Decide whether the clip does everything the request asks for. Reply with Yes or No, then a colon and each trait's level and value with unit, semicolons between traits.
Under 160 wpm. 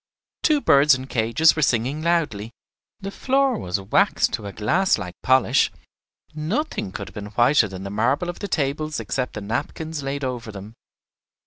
No: average, 175 wpm